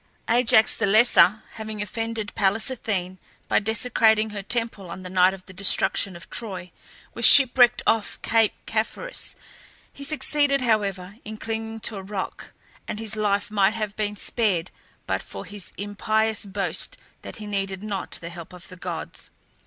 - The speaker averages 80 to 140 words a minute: No, average, 160 wpm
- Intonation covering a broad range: No, narrow, 2.5 semitones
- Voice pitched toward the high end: Yes, high, 210 Hz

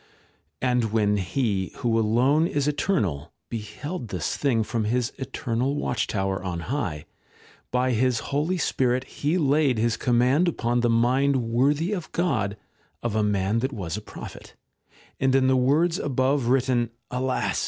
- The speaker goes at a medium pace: Yes, average, 155 wpm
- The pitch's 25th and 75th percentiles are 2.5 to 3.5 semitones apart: No, average, 4.0 semitones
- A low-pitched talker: Yes, low, 125 Hz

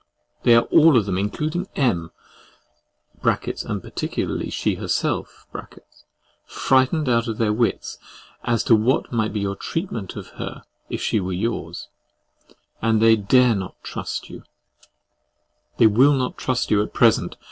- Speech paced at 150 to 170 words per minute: No, average, 140 wpm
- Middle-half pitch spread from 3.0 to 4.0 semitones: Yes, average, 3.6 semitones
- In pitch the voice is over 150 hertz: No, low, 115 Hz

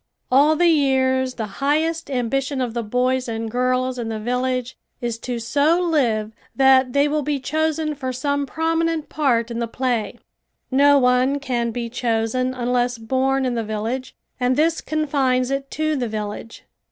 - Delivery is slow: No, average, 165 wpm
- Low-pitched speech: No, very high, 255 Hz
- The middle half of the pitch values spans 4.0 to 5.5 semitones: No, average, 3.0 semitones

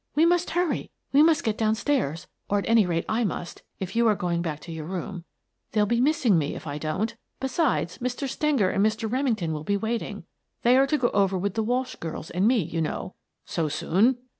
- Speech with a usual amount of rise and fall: No, wide, 6.2 semitones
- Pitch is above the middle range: Yes, high, 215 Hz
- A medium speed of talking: No, fast, 225 wpm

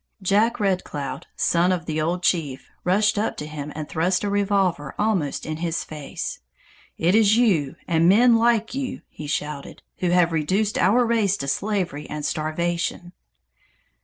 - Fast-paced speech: No, average, 160 wpm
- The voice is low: No, medium, 180 Hz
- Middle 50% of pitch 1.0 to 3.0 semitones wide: No, average, 4.9 semitones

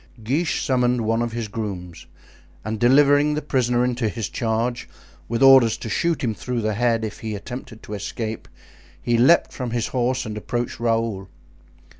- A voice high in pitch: No, low, 120 Hz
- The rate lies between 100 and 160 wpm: No, average, 170 wpm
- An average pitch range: No, narrow, 2.3 semitones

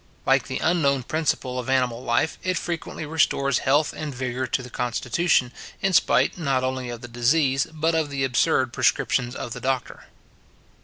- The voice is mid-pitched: No, low, 130 Hz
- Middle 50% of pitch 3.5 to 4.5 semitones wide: Yes, average, 3.9 semitones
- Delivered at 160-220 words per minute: Yes, average, 170 wpm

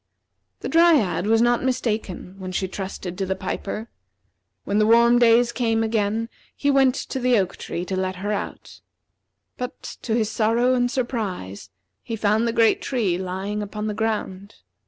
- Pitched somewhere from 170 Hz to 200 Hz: No, high, 220 Hz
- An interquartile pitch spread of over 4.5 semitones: No, average, 3.8 semitones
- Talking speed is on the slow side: No, average, 170 wpm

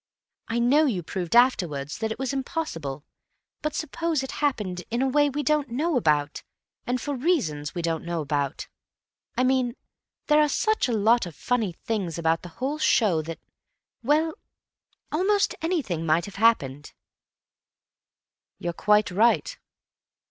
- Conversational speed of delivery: Yes, average, 150 wpm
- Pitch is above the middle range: Yes, high, 230 Hz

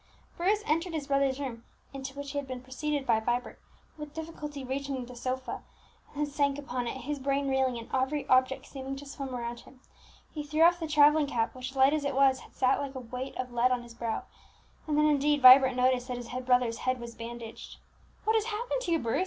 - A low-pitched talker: No, very high, 270 Hz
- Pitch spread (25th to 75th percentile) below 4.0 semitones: Yes, average, 2.7 semitones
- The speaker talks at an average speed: No, fast, 225 wpm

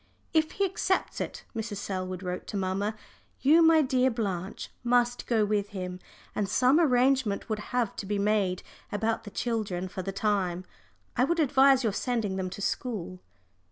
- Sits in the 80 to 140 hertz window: No, high, 215 Hz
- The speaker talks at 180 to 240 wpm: No, average, 170 wpm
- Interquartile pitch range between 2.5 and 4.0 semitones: No, average, 4.7 semitones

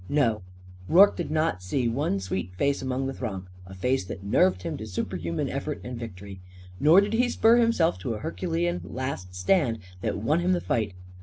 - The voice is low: Yes, low, 125 Hz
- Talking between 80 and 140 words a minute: No, average, 195 wpm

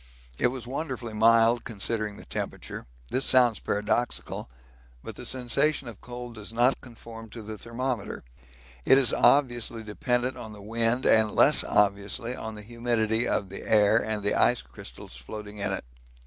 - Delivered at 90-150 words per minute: No, average, 160 wpm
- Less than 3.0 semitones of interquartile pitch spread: Yes, narrow, 2.5 semitones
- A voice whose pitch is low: Yes, low, 115 Hz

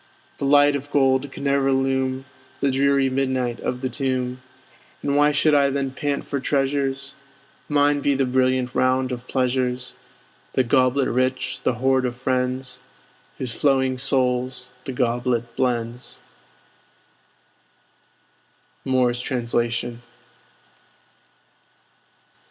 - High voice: No, low, 130 Hz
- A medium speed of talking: No, slow, 115 wpm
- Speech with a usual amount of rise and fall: No, narrow, 1.5 semitones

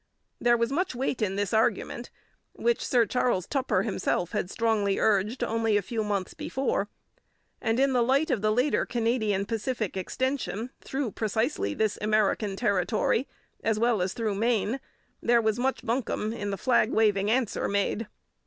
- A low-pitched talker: No, high, 225 Hz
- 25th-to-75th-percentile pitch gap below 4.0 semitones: Yes, average, 3.1 semitones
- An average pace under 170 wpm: Yes, average, 160 wpm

